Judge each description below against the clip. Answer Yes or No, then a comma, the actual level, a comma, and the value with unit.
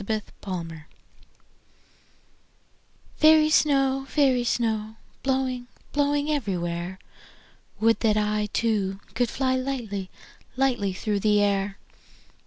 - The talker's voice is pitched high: Yes, high, 225 Hz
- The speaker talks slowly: Yes, slow, 95 wpm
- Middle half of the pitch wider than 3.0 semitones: Yes, average, 4.9 semitones